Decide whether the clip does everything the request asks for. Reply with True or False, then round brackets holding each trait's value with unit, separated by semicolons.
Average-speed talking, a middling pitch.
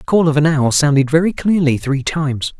False (230 wpm; 150 Hz)